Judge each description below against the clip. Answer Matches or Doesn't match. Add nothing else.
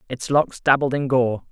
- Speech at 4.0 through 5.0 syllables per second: Matches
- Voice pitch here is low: Matches